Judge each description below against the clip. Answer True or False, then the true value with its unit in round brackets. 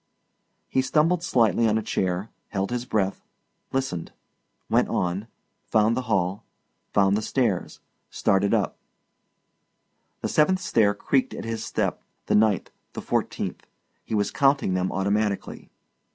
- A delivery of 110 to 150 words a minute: True (135 wpm)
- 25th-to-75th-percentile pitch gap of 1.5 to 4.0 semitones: False (4.4 semitones)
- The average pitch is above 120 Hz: False (110 Hz)